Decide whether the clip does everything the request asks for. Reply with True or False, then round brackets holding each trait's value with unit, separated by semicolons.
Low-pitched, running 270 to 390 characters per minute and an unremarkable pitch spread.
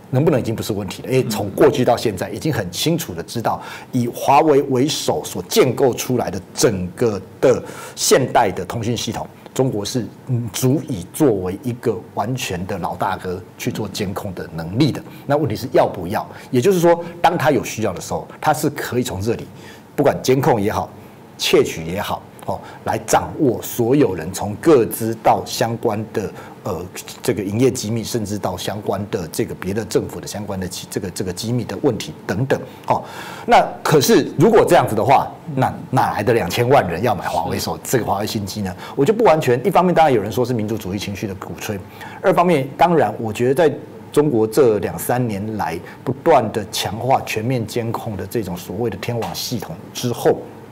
True (115 Hz; 290 characters per minute; 4.1 semitones)